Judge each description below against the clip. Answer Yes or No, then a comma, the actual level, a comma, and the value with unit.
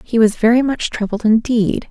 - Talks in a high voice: Yes, high, 225 Hz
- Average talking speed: Yes, average, 190 wpm